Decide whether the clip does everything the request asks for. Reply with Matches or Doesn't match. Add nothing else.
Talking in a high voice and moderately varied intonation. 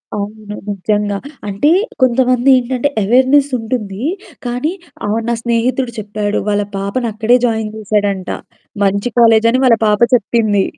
Matches